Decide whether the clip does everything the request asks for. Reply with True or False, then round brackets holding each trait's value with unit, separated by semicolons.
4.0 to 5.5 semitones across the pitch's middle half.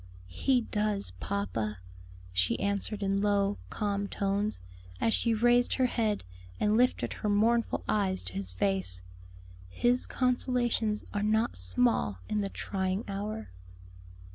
False (3.0 semitones)